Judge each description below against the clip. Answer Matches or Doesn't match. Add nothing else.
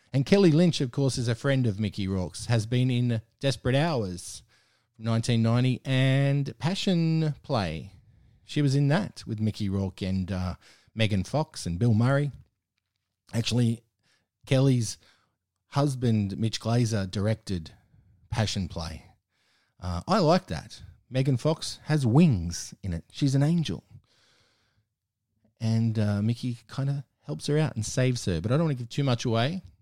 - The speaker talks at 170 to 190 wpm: Doesn't match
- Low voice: Matches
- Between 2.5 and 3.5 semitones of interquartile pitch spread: Doesn't match